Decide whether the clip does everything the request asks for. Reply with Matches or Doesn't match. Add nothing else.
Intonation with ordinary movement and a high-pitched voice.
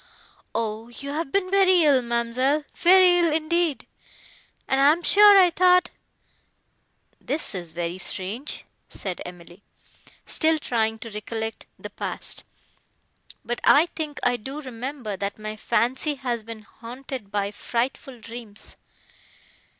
Doesn't match